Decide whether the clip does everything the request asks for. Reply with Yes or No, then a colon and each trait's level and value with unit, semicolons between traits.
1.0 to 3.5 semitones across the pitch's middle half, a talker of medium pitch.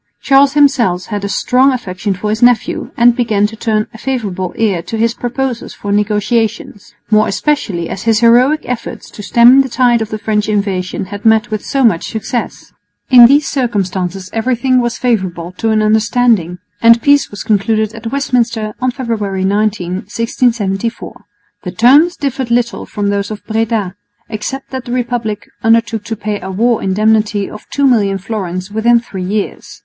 No: average, 3.0 semitones; high, 220 Hz